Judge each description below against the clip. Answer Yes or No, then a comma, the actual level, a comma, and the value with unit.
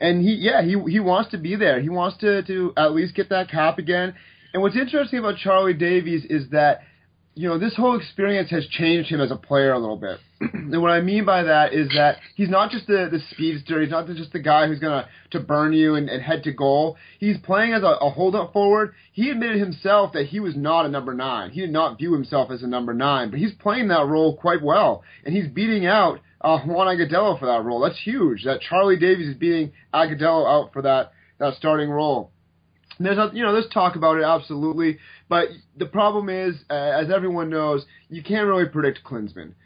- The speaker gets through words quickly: Yes, fast, 225 wpm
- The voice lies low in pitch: No, medium, 165 Hz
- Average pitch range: Yes, average, 4.6 semitones